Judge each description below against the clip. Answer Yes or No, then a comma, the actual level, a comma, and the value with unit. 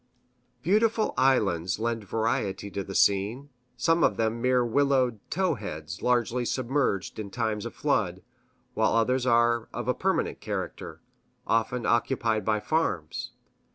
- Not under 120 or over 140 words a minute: Yes, slow, 135 wpm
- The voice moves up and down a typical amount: Yes, average, 3.7 semitones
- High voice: No, low, 115 Hz